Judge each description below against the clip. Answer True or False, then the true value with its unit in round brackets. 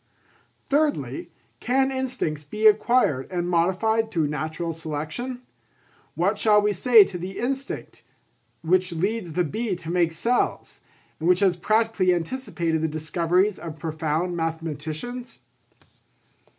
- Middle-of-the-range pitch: True (180 Hz)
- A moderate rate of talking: False (125 wpm)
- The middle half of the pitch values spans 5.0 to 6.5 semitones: True (5.5 semitones)